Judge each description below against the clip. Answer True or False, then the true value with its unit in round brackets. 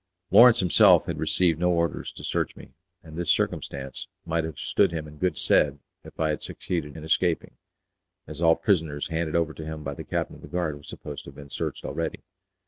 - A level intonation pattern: True (2.2 semitones)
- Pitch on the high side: False (80 Hz)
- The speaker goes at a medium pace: False (215 wpm)